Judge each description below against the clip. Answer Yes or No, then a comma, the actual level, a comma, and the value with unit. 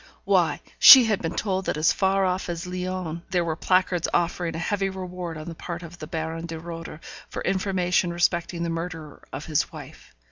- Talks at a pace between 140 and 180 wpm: No, average, 200 wpm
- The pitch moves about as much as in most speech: No, narrow, 2.0 semitones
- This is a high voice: No, medium, 175 Hz